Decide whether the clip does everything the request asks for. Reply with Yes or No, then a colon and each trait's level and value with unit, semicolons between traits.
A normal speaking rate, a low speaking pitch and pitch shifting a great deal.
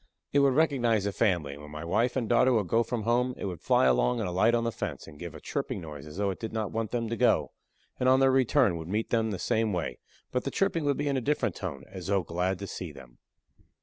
No: fast, 275 wpm; low, 110 Hz; wide, 6.3 semitones